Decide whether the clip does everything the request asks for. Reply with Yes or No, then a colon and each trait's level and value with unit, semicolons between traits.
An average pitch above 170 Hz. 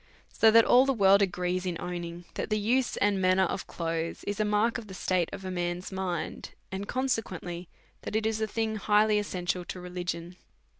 Yes: high, 190 Hz